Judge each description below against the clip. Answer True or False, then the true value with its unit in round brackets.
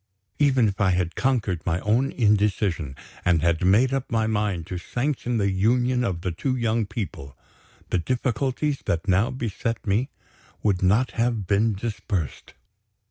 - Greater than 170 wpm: False (155 wpm)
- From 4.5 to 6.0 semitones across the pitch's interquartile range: True (4.8 semitones)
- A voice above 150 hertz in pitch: False (105 Hz)